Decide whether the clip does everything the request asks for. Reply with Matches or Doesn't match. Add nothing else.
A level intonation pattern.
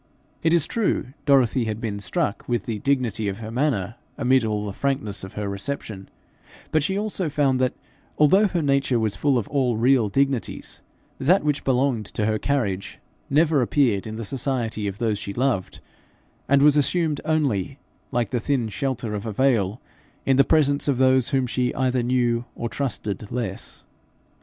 Doesn't match